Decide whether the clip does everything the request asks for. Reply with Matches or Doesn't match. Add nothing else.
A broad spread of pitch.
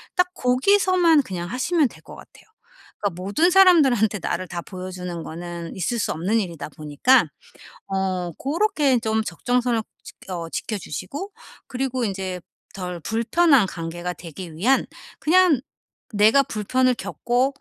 Matches